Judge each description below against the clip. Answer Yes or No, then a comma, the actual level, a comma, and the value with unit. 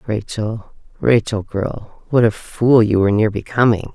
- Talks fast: No, average, 150 wpm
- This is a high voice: No, low, 110 Hz